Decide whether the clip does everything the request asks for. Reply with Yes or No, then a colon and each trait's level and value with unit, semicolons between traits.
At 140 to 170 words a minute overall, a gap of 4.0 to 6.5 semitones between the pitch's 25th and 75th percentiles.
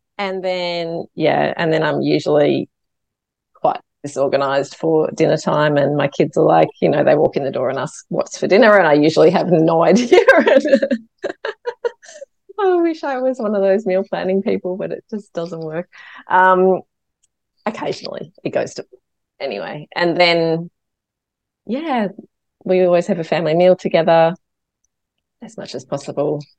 Yes: average, 160 wpm; average, 4.7 semitones